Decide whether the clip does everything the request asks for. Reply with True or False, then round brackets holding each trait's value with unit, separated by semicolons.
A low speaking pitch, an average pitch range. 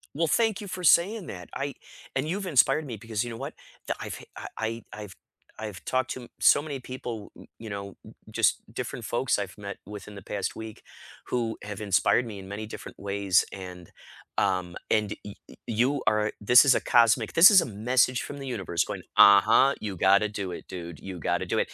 True (110 Hz; 4.7 semitones)